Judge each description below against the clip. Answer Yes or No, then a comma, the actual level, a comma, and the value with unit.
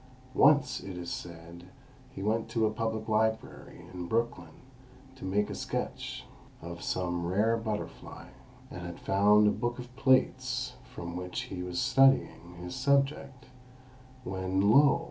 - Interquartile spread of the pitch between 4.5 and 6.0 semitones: Yes, average, 4.9 semitones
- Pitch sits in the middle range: No, low, 105 Hz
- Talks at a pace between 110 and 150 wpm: Yes, average, 145 wpm